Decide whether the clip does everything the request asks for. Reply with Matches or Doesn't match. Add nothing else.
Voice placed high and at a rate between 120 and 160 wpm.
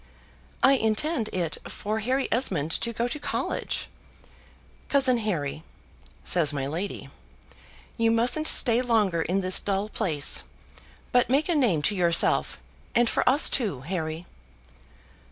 Matches